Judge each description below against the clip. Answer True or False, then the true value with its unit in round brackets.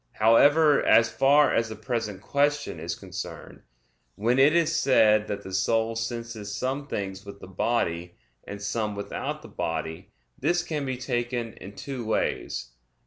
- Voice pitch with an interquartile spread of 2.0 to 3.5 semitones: False (4.9 semitones)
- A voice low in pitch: True (115 Hz)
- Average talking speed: True (155 wpm)